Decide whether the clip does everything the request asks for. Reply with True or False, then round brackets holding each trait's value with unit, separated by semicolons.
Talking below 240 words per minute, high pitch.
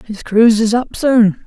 True (205 wpm; 225 Hz)